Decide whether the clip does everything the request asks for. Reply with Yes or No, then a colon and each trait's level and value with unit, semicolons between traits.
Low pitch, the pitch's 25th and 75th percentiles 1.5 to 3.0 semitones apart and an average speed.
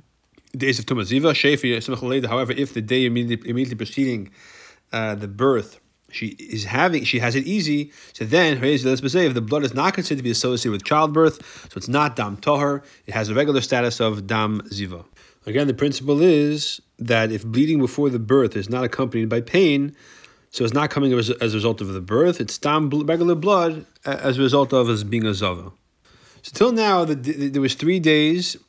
No: low, 130 Hz; average, 4.2 semitones; average, 190 wpm